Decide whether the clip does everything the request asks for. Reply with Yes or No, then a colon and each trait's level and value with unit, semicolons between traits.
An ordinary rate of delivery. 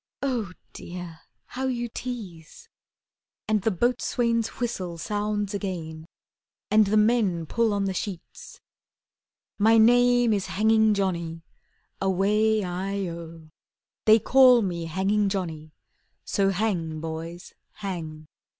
No: slow, 115 wpm